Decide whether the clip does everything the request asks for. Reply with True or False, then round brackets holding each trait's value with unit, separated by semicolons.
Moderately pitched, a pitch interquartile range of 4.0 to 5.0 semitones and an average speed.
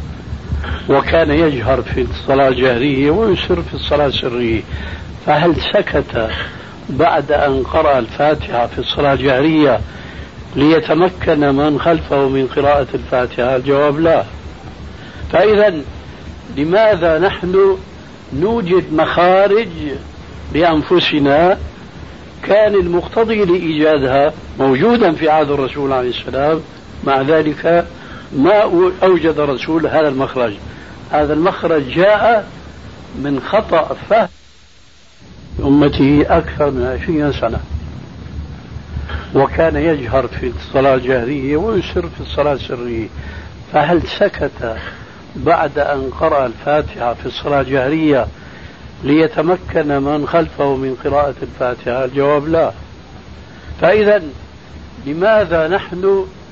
True (145 Hz; 4.4 semitones; 95 wpm)